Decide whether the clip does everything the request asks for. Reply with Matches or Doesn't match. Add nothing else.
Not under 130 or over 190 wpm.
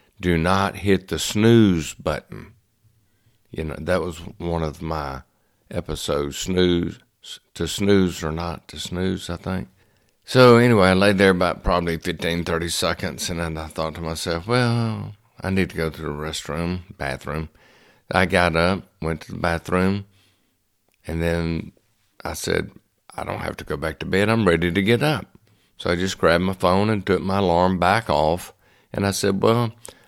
Matches